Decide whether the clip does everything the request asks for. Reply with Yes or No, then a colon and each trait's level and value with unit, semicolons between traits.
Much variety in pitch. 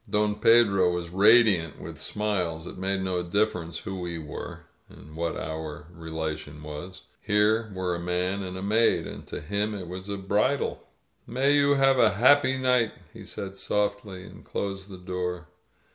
No: average, 3.3 semitones